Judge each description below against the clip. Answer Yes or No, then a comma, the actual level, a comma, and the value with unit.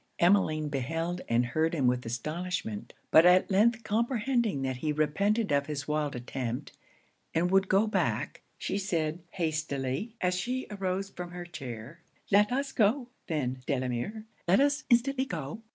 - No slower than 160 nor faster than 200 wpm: No, average, 150 wpm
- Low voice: No, medium, 175 Hz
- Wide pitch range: Yes, wide, 6.7 semitones